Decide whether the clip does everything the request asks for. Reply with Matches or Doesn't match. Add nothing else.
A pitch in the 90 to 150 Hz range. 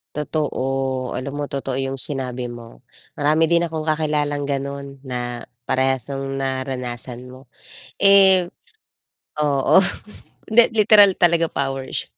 Matches